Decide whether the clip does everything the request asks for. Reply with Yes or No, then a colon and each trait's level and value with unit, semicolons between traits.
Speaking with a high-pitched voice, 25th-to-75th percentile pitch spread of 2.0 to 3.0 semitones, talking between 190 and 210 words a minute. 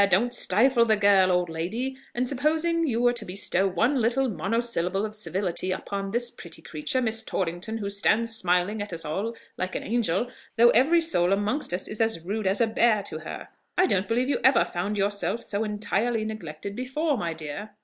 No: high, 215 Hz; average, 4.2 semitones; average, 195 wpm